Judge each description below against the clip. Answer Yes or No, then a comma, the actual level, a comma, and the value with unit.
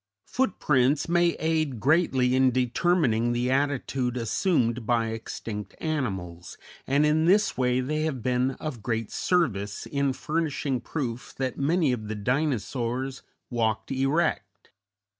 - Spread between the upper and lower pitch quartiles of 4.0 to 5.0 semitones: Yes, average, 4.5 semitones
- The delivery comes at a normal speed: No, slow, 125 wpm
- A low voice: Yes, low, 130 Hz